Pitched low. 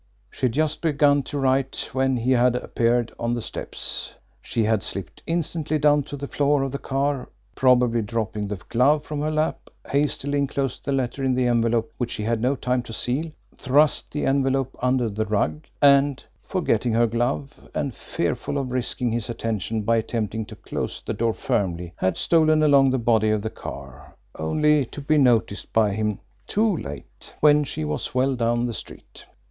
Yes: low, 125 Hz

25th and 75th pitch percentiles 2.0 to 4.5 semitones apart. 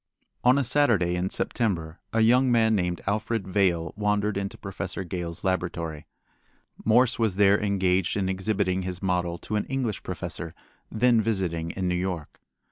Yes: average, 3.6 semitones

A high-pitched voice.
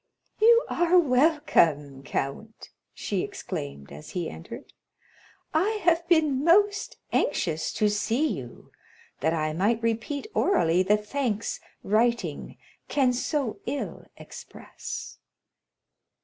Yes: high, 235 Hz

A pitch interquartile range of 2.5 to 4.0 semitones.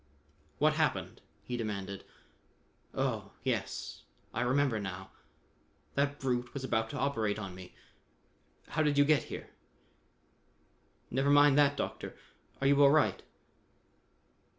No: average, 4.8 semitones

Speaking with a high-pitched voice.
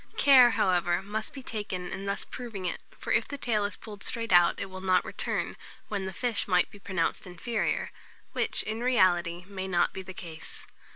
Yes: high, 195 Hz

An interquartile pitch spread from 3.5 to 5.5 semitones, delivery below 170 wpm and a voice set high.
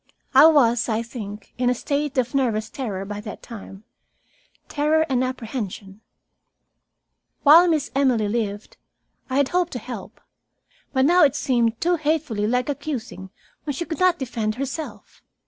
Yes: average, 5.0 semitones; average, 150 wpm; very high, 255 Hz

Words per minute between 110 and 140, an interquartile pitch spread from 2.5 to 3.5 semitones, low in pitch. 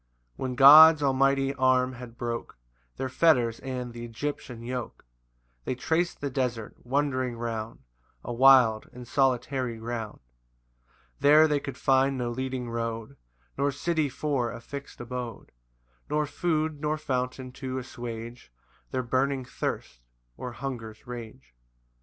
Yes: slow, 135 wpm; average, 2.8 semitones; low, 130 Hz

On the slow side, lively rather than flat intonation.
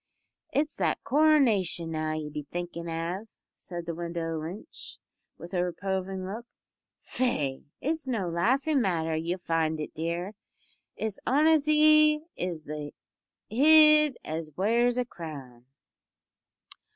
Yes: slow, 120 wpm; wide, 7.8 semitones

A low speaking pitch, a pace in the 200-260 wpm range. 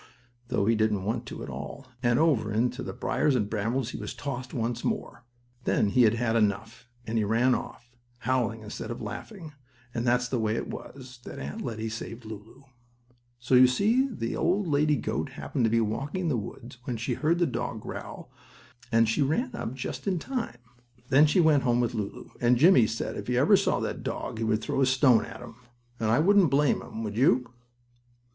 Yes: low, 120 Hz; fast, 205 wpm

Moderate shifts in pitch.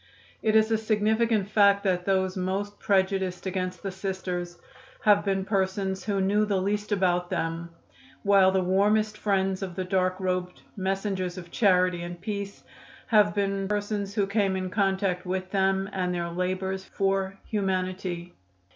No: narrow, 1.6 semitones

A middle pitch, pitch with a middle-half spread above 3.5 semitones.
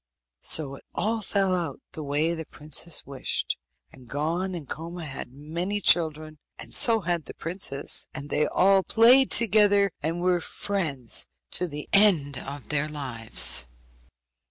Yes: medium, 160 Hz; average, 4.8 semitones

